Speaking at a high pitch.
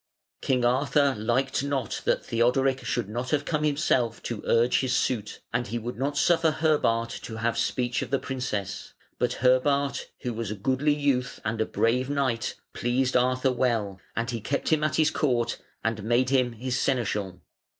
No: low, 125 Hz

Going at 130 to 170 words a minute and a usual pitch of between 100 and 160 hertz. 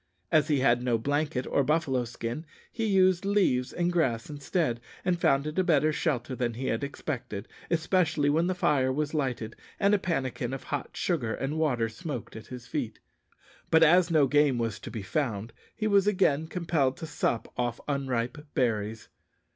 No: average, 180 wpm; medium, 140 Hz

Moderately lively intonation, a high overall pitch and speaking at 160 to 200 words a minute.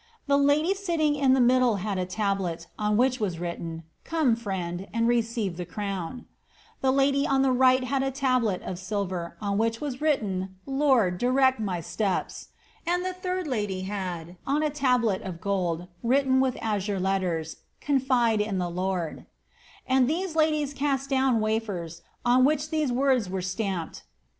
No: wide, 6.3 semitones; high, 230 Hz; average, 175 wpm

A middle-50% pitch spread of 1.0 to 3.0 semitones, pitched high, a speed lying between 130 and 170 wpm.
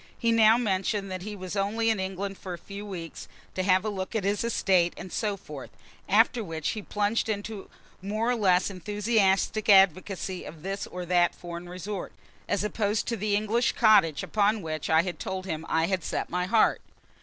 No: average, 2.7 semitones; high, 195 Hz; average, 190 wpm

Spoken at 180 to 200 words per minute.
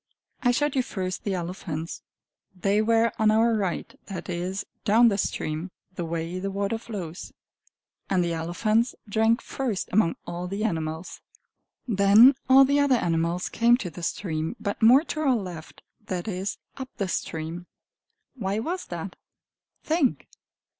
No: average, 155 wpm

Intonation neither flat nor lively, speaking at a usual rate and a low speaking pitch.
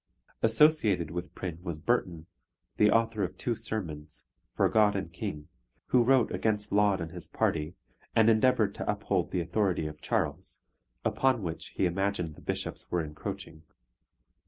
Yes: average, 5.0 semitones; average, 155 wpm; very low, 95 Hz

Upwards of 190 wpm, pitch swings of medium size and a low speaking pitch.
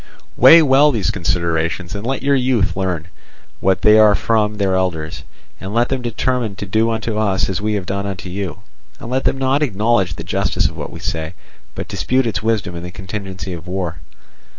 Yes: average, 200 wpm; average, 4.0 semitones; low, 100 Hz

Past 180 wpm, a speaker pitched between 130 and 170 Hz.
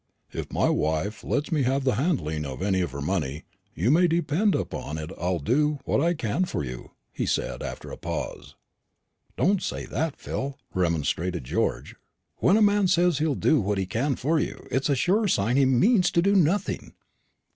Yes: average, 190 wpm; low, 135 Hz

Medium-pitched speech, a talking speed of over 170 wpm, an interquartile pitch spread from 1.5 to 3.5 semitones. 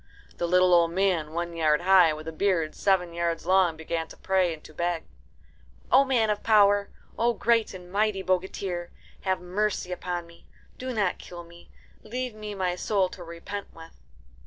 Yes: medium, 180 Hz; average, 180 wpm; average, 3.0 semitones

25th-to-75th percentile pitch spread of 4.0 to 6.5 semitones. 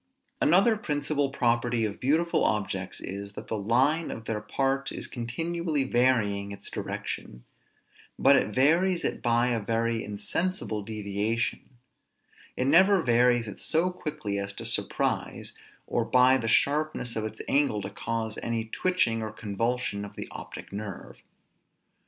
Yes: average, 5.1 semitones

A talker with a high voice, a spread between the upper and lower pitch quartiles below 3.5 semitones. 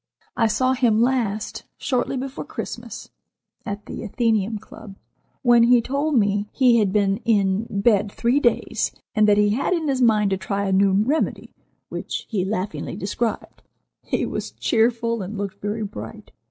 Yes: high, 220 Hz; average, 3.1 semitones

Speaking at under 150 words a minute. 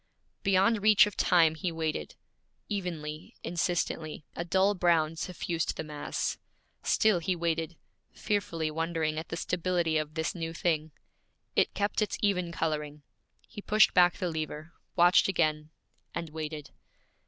Yes: average, 140 wpm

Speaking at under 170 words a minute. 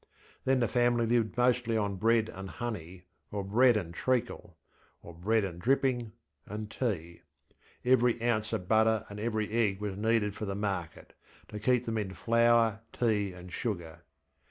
Yes: average, 160 wpm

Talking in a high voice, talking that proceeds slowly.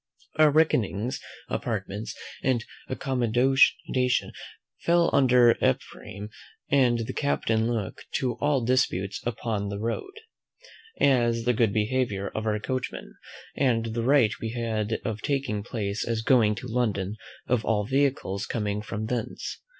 No: low, 115 Hz; slow, 130 wpm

